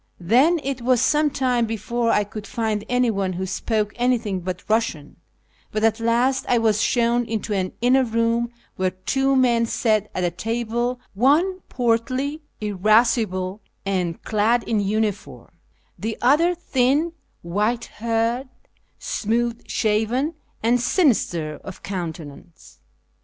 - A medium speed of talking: No, slow, 130 wpm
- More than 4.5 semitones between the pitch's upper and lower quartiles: No, average, 3.2 semitones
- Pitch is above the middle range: Yes, high, 230 Hz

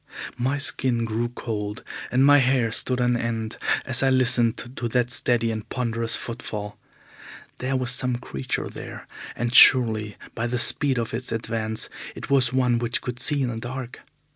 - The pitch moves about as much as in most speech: No, narrow, 1.9 semitones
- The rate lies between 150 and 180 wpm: Yes, average, 170 wpm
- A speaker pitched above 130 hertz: No, low, 120 Hz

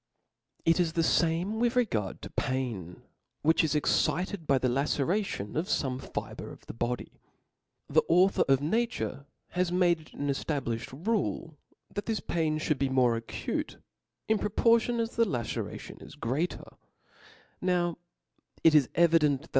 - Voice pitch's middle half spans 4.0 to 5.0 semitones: No, wide, 5.5 semitones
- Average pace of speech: Yes, average, 155 wpm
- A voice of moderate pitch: Yes, medium, 160 Hz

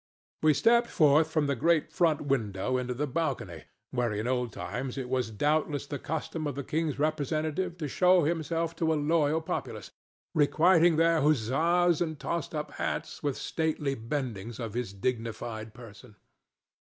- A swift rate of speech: No, average, 160 wpm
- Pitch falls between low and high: Yes, medium, 145 Hz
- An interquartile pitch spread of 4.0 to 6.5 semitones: Yes, average, 4.4 semitones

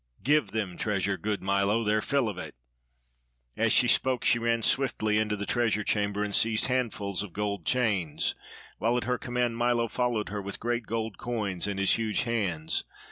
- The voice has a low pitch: Yes, low, 110 Hz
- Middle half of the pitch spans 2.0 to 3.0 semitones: Yes, average, 2.7 semitones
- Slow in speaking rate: No, average, 185 wpm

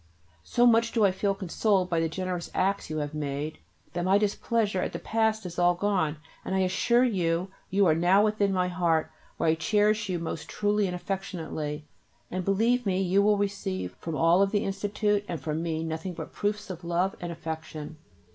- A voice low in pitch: No, medium, 185 Hz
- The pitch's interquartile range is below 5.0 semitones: Yes, average, 3.7 semitones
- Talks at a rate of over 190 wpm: Yes, average, 200 wpm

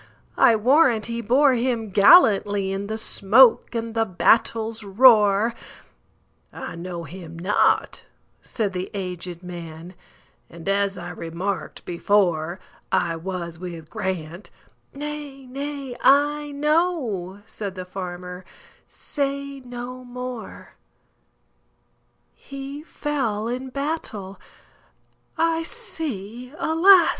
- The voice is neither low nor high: No, high, 215 Hz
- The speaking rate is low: Yes, slow, 85 wpm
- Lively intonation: Yes, wide, 6.5 semitones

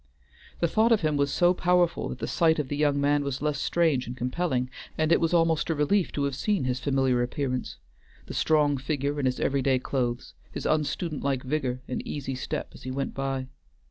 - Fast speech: Yes, fast, 215 wpm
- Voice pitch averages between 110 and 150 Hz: Yes, medium, 140 Hz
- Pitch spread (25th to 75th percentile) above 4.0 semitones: No, average, 3.3 semitones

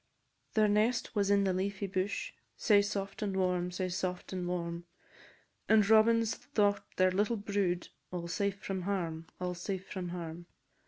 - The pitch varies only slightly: Yes, narrow, 2.2 semitones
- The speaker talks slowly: No, average, 165 wpm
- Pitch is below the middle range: No, high, 190 Hz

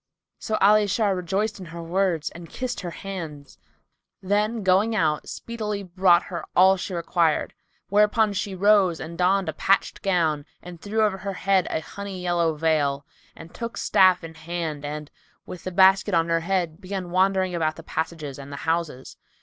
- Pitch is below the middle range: No, medium, 180 Hz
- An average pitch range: Yes, average, 3.2 semitones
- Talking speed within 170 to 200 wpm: Yes, average, 175 wpm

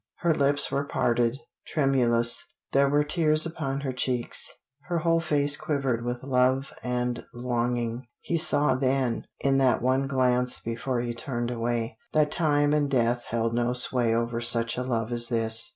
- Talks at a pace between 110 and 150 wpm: No, average, 165 wpm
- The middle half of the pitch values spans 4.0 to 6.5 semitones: No, average, 3.0 semitones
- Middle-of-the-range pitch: No, low, 125 Hz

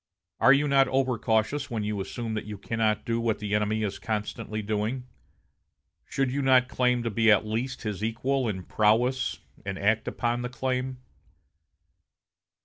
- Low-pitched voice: Yes, low, 115 Hz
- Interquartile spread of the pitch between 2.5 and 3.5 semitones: Yes, average, 3.2 semitones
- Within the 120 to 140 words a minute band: No, average, 165 wpm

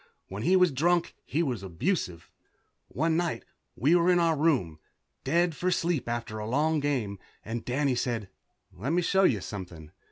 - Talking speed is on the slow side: No, average, 170 wpm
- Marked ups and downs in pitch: Yes, wide, 7.7 semitones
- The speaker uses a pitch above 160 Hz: No, medium, 140 Hz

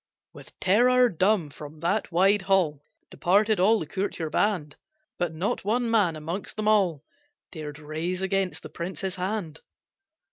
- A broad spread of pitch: No, average, 4.3 semitones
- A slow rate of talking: No, average, 150 wpm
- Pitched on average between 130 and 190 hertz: Yes, medium, 185 Hz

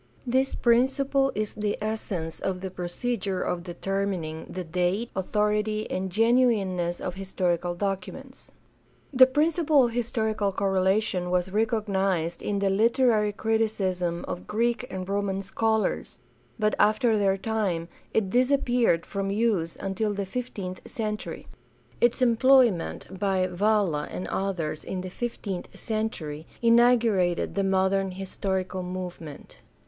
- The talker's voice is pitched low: No, high, 200 Hz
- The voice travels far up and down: No, average, 3.5 semitones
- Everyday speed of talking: No, slow, 125 wpm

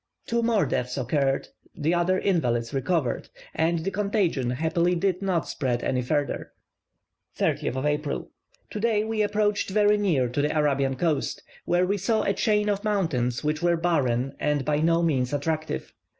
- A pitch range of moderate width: No, wide, 6.2 semitones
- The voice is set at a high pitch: No, medium, 160 Hz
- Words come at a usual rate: Yes, average, 160 wpm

